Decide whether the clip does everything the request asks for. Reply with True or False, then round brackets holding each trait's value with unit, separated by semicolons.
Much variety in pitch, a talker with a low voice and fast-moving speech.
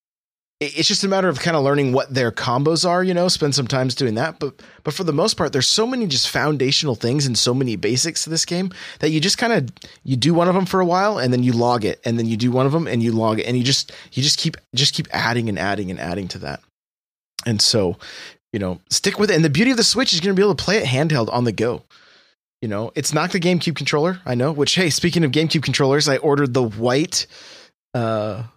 False (5.7 semitones; 145 Hz; 265 wpm)